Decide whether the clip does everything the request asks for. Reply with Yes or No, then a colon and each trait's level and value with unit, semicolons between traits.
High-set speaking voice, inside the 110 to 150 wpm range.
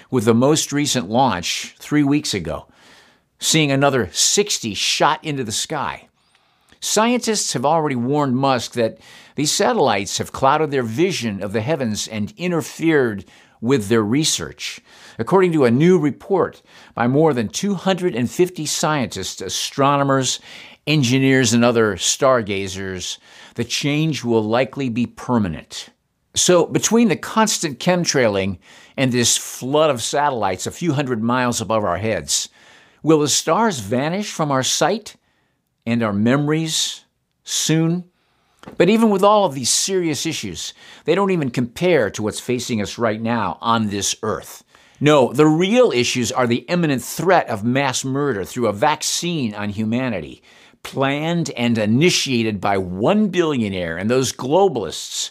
No: low, 130 Hz; average, 140 wpm